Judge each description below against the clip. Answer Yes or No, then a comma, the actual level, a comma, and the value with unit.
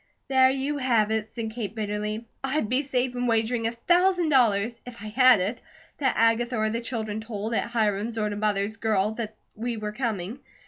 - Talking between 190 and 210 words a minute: Yes, average, 195 wpm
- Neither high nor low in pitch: No, high, 225 Hz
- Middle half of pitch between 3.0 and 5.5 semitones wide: No, narrow, 2.6 semitones